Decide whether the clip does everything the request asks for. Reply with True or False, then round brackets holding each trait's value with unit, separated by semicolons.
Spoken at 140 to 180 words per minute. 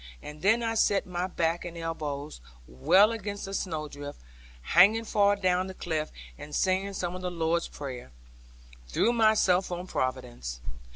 True (155 wpm)